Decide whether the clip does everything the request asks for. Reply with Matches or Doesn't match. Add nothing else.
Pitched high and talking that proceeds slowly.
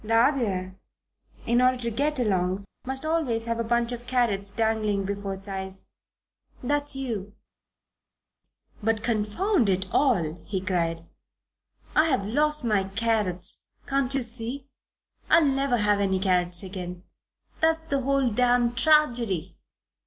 Matches